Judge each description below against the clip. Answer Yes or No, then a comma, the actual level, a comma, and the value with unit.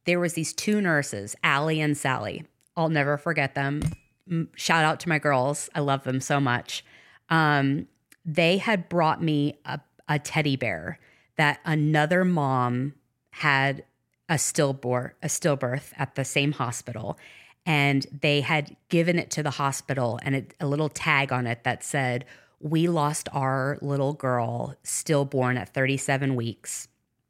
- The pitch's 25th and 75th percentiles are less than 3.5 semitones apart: Yes, average, 2.8 semitones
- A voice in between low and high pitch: Yes, medium, 145 Hz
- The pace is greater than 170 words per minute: No, average, 150 wpm